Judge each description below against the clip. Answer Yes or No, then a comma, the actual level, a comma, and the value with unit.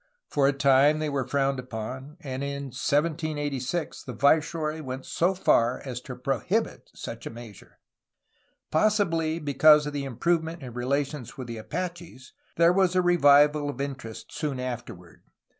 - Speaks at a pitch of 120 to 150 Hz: Yes, medium, 140 Hz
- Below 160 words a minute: Yes, average, 150 wpm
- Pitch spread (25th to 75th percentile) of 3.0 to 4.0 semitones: Yes, average, 3.5 semitones